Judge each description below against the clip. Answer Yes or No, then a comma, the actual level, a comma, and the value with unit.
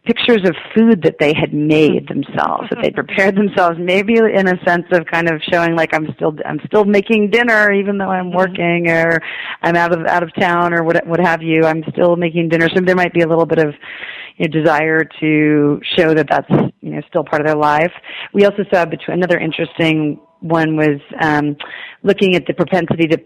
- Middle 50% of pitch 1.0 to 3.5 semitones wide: Yes, average, 2.7 semitones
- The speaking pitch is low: No, medium, 170 Hz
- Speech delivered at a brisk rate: Yes, fast, 215 wpm